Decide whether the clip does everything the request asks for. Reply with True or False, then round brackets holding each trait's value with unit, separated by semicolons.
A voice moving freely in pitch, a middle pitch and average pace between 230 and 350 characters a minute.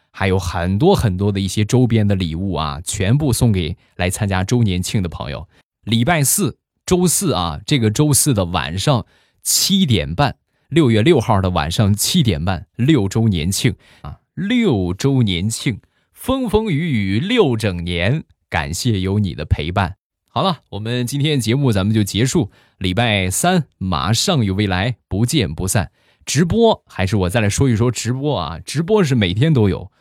False (6.6 semitones; 110 Hz; 245 characters per minute)